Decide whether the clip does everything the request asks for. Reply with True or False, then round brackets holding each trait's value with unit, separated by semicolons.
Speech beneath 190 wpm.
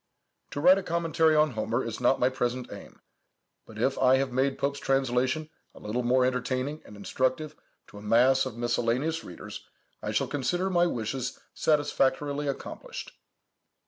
True (160 wpm)